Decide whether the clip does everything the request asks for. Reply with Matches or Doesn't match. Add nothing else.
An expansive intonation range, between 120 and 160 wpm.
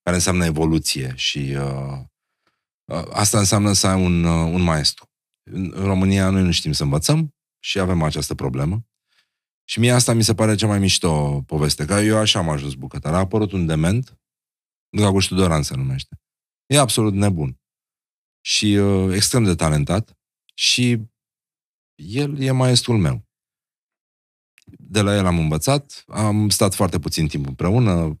Matches